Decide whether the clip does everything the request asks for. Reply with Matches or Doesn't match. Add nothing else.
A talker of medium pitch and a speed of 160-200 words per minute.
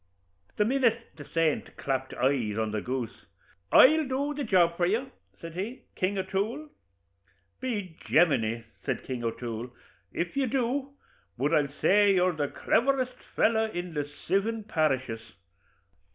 Doesn't match